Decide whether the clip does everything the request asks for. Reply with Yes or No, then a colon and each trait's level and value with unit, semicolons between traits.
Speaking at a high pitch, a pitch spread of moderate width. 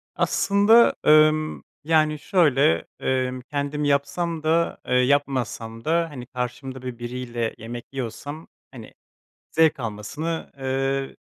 No: medium, 140 Hz; average, 3.7 semitones